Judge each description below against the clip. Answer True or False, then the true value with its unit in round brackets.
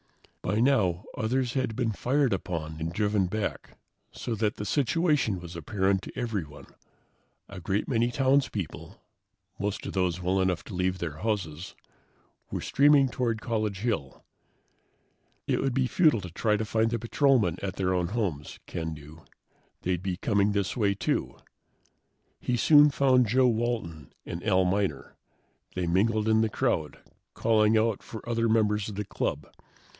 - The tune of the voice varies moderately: True (4.3 semitones)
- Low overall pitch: True (105 Hz)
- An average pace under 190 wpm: True (160 wpm)